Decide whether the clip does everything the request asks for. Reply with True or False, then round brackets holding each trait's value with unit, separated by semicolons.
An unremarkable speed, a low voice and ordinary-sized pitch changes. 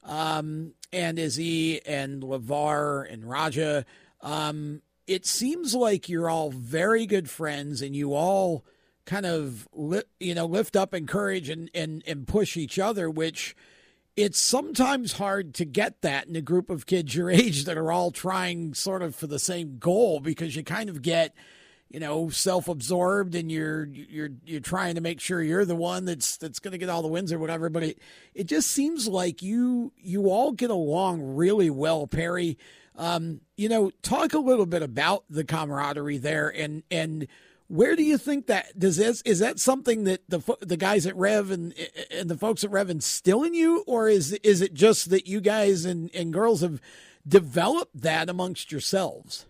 False (185 wpm; 175 Hz; 4.1 semitones)